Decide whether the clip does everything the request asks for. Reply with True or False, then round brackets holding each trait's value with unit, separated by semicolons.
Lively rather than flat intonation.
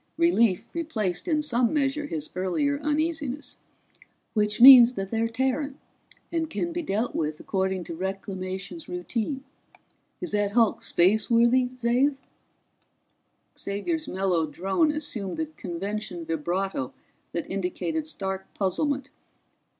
True (7.4 semitones)